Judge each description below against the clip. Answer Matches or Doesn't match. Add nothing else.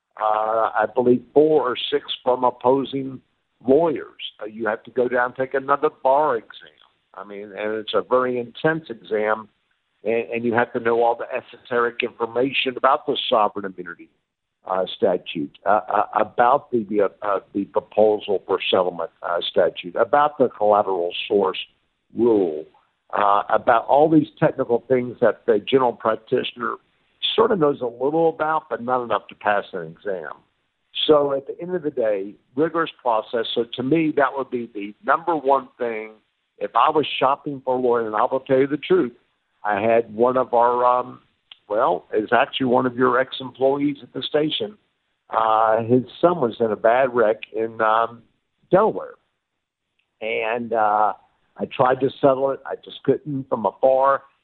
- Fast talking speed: Doesn't match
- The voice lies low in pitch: Matches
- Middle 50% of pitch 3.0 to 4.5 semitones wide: Matches